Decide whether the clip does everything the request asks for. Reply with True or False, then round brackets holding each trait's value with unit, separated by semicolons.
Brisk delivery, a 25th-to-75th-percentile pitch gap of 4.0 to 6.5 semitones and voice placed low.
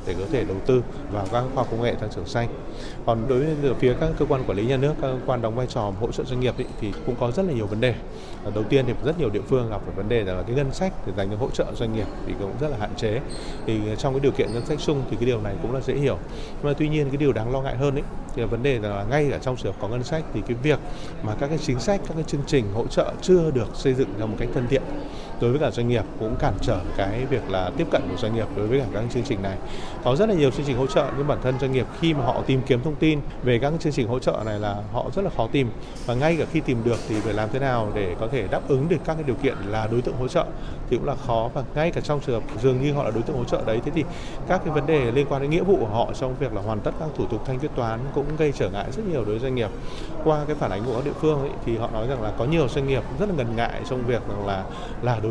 True (320 wpm; 4.3 semitones; 130 Hz)